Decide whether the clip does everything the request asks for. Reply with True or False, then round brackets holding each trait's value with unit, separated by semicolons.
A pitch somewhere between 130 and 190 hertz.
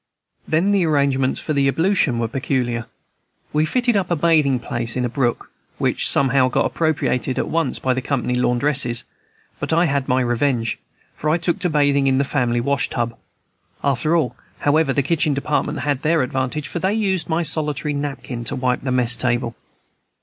True (140 Hz)